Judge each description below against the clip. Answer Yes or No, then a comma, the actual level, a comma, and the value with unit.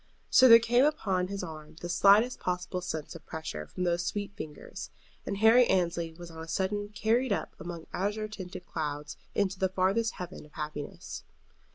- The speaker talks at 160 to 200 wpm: Yes, average, 180 wpm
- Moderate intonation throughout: Yes, average, 4.1 semitones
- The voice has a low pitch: No, medium, 185 Hz